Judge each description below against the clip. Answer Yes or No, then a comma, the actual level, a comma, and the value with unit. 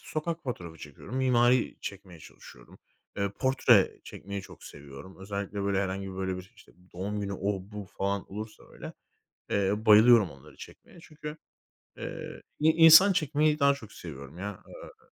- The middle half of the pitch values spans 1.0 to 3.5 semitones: No, wide, 5.5 semitones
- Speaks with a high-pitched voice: No, low, 100 Hz